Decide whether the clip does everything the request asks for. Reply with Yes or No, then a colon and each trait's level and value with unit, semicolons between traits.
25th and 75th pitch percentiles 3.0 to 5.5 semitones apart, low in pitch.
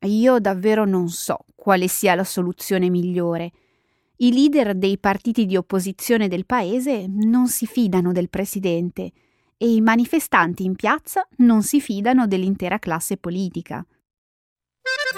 No: average, 4.6 semitones; high, 195 Hz